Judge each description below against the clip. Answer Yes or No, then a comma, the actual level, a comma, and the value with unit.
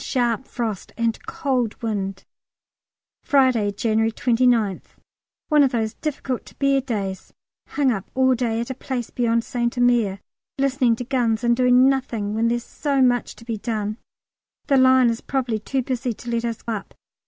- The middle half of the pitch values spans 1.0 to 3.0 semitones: Yes, narrow, 2.6 semitones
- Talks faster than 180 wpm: No, average, 165 wpm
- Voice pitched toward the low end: No, high, 240 Hz